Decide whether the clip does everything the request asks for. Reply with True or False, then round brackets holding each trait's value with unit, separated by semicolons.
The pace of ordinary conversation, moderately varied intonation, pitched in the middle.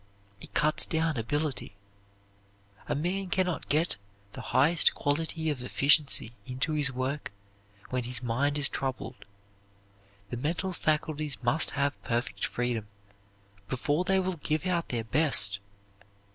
False (130 wpm; 4.2 semitones; 145 Hz)